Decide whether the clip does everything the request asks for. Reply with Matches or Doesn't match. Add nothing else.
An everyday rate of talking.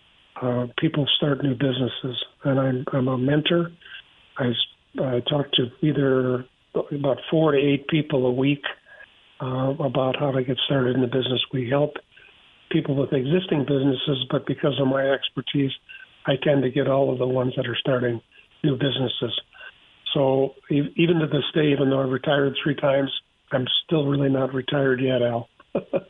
Matches